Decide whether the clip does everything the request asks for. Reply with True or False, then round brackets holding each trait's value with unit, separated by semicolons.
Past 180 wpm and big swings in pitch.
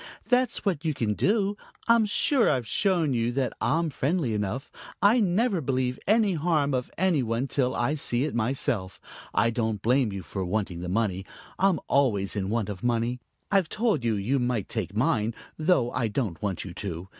True (190 wpm; 7.5 semitones)